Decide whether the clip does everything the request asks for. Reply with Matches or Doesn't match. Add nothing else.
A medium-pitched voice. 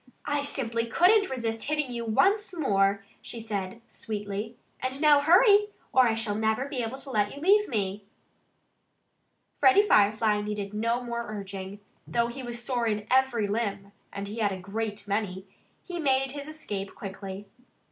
Doesn't match